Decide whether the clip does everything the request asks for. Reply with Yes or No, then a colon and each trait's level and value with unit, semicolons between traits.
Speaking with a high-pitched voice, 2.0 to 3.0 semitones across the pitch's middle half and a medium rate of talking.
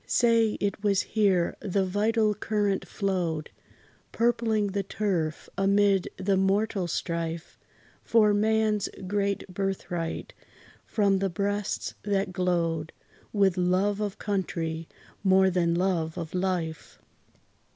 No: high, 195 Hz; narrow, 2.5 semitones; slow, 110 wpm